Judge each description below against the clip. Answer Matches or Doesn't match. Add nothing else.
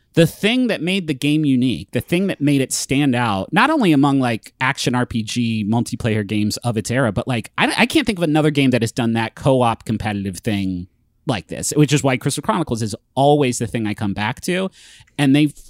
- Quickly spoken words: Matches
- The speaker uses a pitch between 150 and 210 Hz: Doesn't match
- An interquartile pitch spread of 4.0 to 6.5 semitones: Matches